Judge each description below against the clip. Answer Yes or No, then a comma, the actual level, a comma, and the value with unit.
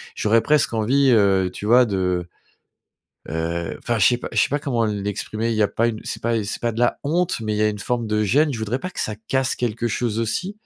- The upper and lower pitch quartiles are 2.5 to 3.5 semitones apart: Yes, average, 2.9 semitones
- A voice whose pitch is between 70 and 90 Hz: No, low, 115 Hz